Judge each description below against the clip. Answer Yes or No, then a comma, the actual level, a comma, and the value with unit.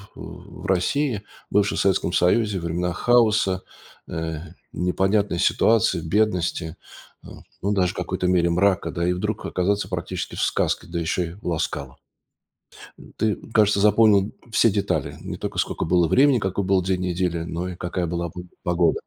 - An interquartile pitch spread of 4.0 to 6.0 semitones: No, average, 2.9 semitones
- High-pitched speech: No, very low, 90 Hz